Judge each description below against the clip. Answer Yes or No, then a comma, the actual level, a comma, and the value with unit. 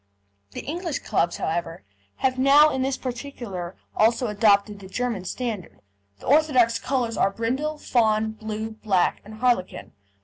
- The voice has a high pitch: Yes, high, 230 Hz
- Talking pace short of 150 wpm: Yes, average, 140 wpm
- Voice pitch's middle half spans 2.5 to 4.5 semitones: Yes, average, 4.1 semitones